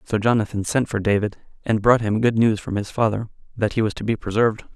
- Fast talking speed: Yes, fast, 240 wpm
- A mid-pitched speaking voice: No, low, 110 Hz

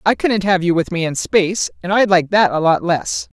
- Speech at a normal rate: No, fast, 265 wpm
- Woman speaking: Yes, female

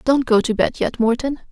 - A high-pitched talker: Yes, high, 245 Hz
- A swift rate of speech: Yes, fast, 240 wpm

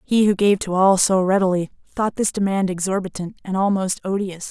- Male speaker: No, female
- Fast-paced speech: No, average, 185 wpm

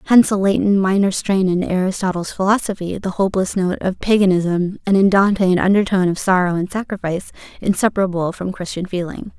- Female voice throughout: Yes, female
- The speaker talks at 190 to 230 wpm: No, average, 165 wpm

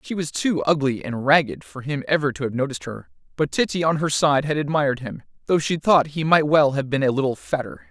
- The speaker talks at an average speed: No, fast, 245 wpm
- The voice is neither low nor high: Yes, medium, 145 Hz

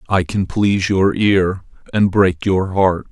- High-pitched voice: No, very low, 95 Hz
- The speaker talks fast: No, average, 175 wpm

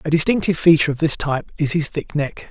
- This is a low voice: No, medium, 155 Hz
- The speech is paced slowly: No, fast, 240 wpm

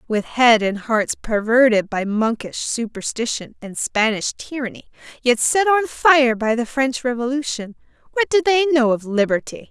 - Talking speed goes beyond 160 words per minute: No, average, 155 wpm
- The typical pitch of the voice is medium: No, high, 245 Hz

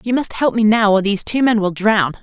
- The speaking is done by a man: No, female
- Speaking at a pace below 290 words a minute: No, fast, 295 wpm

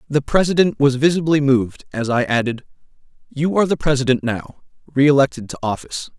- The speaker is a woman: No, male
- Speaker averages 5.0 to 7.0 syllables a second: Yes, 5.8 syllables/s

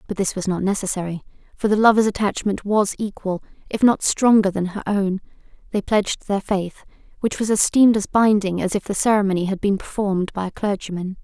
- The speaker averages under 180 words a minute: No, average, 190 wpm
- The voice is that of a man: No, female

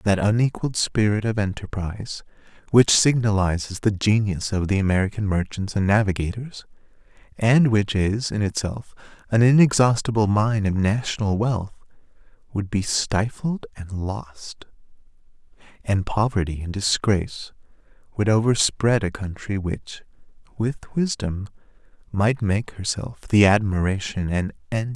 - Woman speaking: No, male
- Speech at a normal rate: No, slow, 125 wpm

